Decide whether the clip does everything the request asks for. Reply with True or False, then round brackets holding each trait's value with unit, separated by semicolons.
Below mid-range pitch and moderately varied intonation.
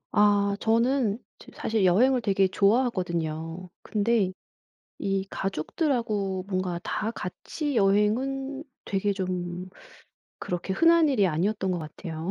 False (200 Hz; 4.1 semitones)